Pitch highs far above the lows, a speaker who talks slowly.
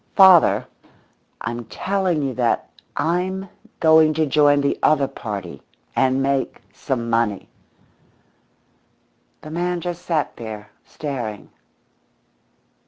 Yes: wide, 6.3 semitones; slow, 105 wpm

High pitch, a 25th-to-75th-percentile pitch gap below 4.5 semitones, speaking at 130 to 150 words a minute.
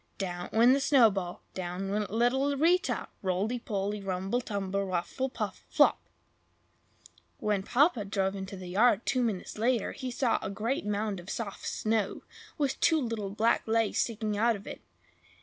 No: high, 215 Hz; average, 3.8 semitones; average, 160 wpm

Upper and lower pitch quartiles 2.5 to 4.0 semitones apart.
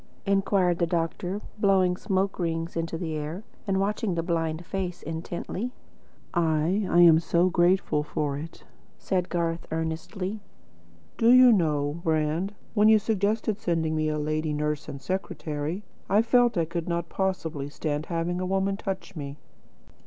Yes: average, 3.4 semitones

